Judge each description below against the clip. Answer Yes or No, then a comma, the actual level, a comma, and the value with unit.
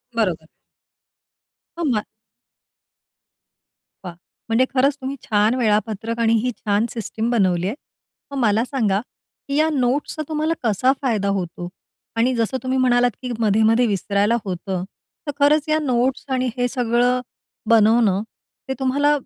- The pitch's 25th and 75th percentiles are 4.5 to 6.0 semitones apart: No, average, 3.7 semitones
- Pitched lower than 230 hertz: No, high, 235 Hz